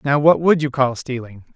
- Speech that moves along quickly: Yes, fast, 230 wpm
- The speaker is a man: Yes, male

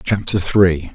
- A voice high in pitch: No, very low, 90 Hz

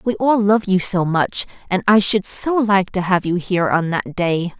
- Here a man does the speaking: No, female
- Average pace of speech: No, fast, 235 wpm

